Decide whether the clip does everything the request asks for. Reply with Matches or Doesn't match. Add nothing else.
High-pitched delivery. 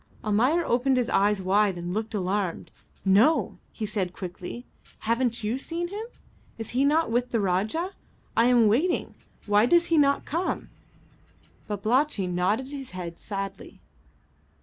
Matches